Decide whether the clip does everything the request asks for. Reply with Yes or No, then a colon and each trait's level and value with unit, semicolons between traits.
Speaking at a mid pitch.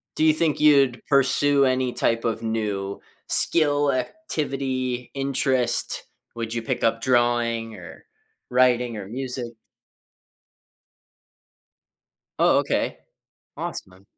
No: low, 125 Hz